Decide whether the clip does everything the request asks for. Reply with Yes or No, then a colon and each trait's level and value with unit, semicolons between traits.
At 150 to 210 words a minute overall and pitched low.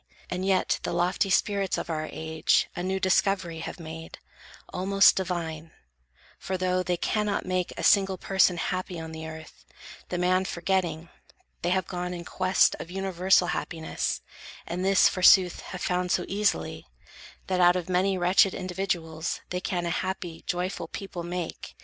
No: average, 160 wpm; medium, 180 Hz